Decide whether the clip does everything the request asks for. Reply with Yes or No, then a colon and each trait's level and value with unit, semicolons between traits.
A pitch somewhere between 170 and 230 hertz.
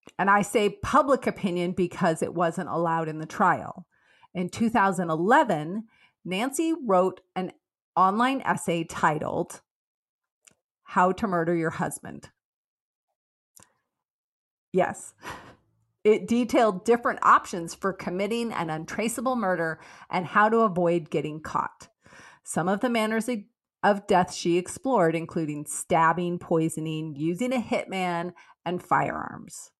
Yes: medium, 185 Hz